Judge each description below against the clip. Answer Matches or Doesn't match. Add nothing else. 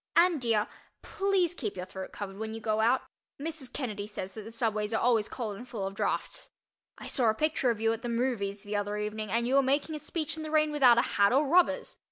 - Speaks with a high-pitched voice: Matches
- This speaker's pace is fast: Matches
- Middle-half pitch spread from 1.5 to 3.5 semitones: Doesn't match